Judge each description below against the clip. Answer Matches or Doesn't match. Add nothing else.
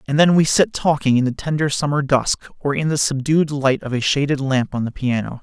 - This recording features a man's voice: Matches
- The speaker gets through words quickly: Matches